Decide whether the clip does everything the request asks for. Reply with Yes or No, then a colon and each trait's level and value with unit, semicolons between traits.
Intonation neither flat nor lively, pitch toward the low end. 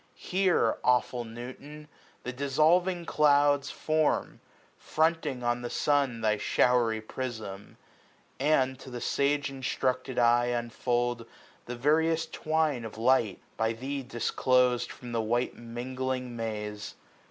Yes: average, 3.3 semitones; low, 125 Hz